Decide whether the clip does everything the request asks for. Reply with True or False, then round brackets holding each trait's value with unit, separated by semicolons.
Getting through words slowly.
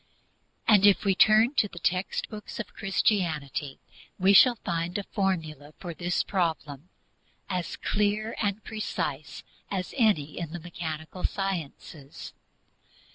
True (130 wpm)